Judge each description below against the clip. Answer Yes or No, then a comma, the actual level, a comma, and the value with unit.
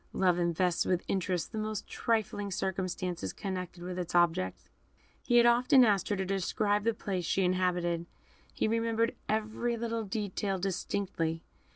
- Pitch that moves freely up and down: No, average, 3.4 semitones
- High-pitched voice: Yes, high, 195 Hz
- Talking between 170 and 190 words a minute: No, average, 150 wpm